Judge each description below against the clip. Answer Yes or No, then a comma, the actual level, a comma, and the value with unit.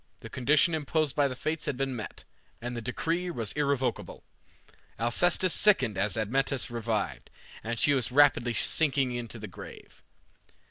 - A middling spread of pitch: Yes, average, 3.9 semitones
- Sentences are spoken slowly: No, average, 150 wpm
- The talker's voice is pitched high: No, low, 130 Hz